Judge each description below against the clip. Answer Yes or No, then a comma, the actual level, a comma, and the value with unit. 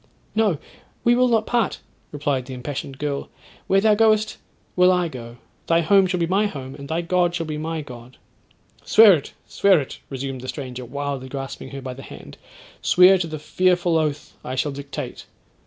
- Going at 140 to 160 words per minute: No, average, 185 wpm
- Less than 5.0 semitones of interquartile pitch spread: No, wide, 5.4 semitones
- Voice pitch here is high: No, medium, 155 Hz